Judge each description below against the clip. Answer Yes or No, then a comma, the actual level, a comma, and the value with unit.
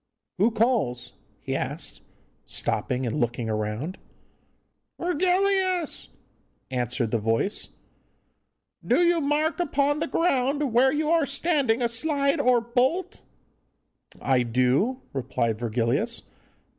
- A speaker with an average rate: No, slow, 105 wpm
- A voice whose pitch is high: Yes, high, 245 Hz